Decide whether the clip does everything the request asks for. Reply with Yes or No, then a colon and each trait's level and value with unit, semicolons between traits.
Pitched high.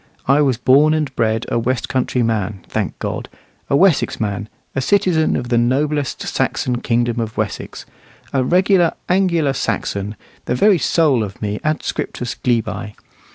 No: low, 125 Hz